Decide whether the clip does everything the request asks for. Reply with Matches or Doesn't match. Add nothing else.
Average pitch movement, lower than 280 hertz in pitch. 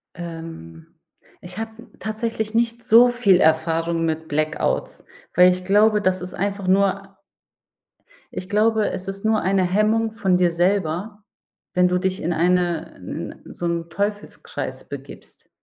Matches